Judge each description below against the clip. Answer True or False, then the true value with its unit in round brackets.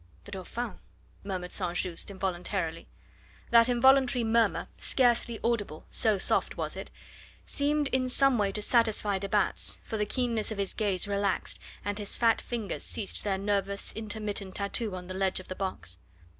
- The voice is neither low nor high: False (205 Hz)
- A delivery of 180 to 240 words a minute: False (165 wpm)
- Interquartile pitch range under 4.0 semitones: True (3.4 semitones)